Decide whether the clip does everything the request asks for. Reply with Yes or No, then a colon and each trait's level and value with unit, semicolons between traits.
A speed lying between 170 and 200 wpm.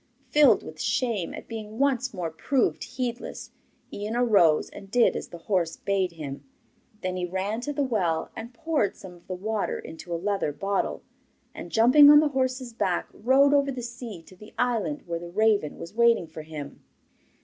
Yes: average, 185 wpm